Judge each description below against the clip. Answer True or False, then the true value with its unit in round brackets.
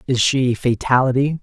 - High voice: False (125 Hz)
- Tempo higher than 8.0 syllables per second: False (4.8 syllables/s)